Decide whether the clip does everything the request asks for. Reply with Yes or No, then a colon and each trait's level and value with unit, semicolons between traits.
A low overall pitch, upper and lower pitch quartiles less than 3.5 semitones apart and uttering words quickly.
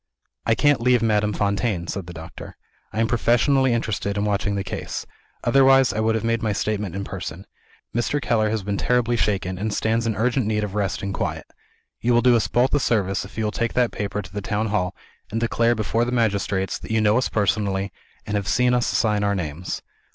Yes: low, 105 Hz; average, 2.8 semitones; fast, 220 wpm